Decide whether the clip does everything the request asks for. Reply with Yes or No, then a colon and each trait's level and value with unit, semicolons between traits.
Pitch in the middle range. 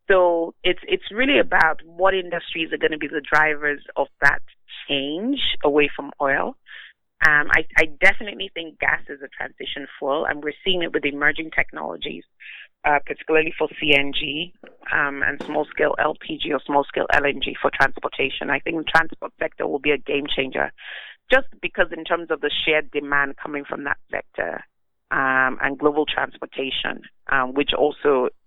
Yes: medium, 155 Hz